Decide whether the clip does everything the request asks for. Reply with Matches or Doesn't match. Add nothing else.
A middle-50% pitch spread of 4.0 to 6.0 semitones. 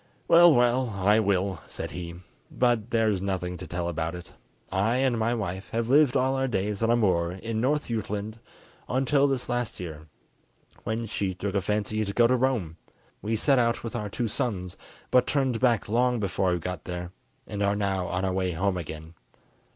Matches